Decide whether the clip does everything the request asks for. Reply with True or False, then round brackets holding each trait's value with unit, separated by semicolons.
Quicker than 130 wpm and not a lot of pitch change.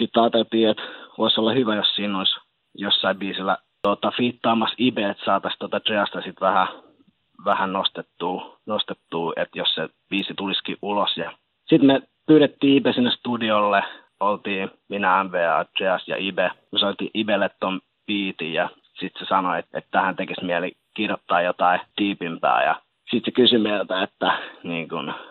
False (155 wpm; 3.5 semitones)